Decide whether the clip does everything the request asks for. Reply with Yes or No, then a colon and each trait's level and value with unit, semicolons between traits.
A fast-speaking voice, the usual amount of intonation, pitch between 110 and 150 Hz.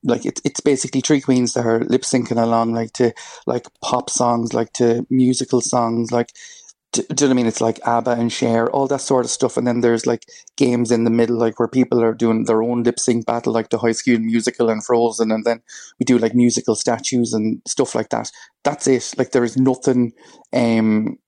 No: fast, 225 wpm; narrow, 1.5 semitones; low, 120 Hz